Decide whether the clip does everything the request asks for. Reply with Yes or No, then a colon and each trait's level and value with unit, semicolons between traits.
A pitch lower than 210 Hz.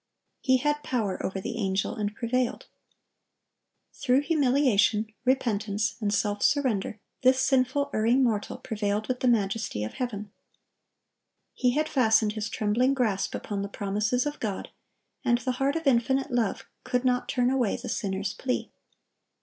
No: high, 235 Hz